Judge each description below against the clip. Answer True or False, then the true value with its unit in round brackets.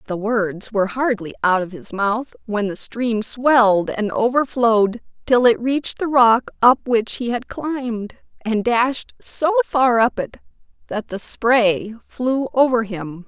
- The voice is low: False (230 Hz)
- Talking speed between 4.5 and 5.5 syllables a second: False (3.9 syllables/s)